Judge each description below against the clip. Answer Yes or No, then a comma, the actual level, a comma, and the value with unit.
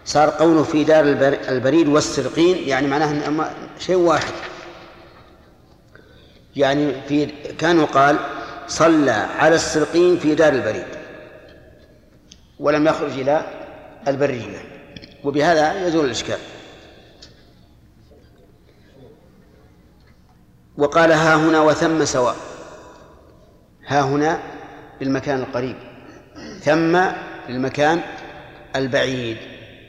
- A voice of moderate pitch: Yes, medium, 145 Hz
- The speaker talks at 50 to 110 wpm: Yes, average, 80 wpm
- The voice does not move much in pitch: No, average, 3.8 semitones